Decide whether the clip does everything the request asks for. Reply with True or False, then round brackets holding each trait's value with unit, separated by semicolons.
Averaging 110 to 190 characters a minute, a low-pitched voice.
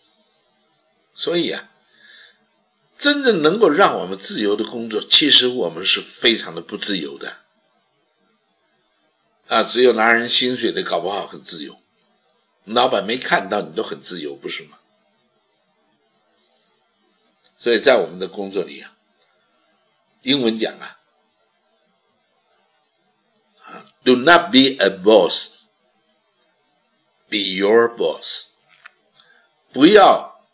True (185 characters per minute; 125 Hz)